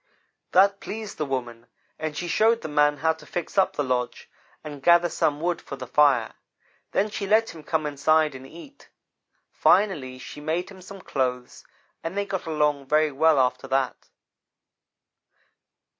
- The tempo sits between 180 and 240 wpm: No, average, 165 wpm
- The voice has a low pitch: No, medium, 155 Hz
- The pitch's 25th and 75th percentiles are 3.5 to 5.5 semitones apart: Yes, average, 4.9 semitones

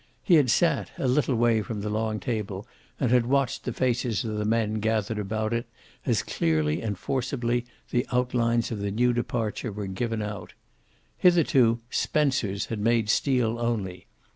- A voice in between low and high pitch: No, low, 115 Hz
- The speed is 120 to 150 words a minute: No, average, 165 wpm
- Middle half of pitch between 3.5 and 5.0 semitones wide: No, average, 2.7 semitones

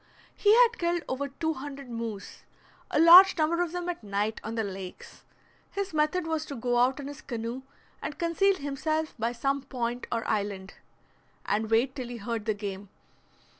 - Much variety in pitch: Yes, wide, 6.1 semitones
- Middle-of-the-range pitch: No, very high, 265 Hz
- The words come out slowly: No, average, 180 wpm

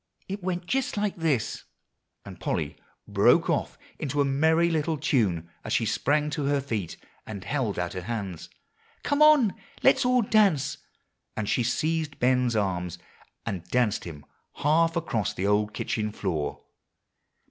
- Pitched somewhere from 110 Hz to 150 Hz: Yes, low, 135 Hz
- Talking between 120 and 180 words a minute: Yes, average, 155 wpm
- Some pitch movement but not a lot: No, wide, 8.1 semitones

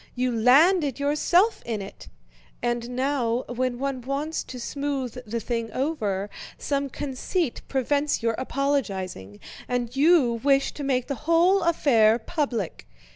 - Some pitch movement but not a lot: Yes, average, 3.6 semitones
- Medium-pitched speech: No, very high, 260 Hz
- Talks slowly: Yes, slow, 130 wpm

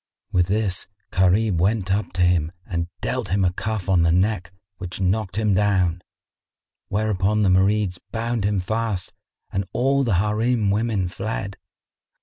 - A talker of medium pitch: No, low, 100 Hz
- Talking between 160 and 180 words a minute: No, average, 150 wpm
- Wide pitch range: No, average, 3.0 semitones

